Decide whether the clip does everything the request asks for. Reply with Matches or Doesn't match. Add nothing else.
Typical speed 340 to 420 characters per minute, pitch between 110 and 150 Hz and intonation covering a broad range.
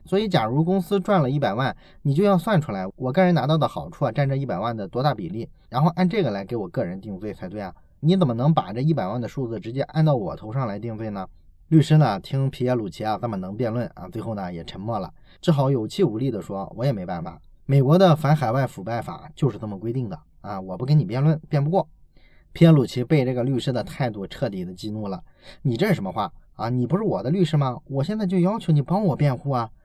Matches